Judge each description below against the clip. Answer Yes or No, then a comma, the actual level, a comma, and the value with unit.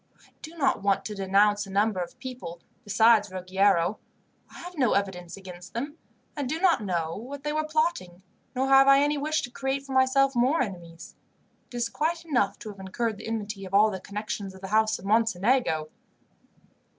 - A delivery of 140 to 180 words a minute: No, average, 195 wpm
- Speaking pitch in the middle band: No, high, 220 Hz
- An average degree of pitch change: No, wide, 5.8 semitones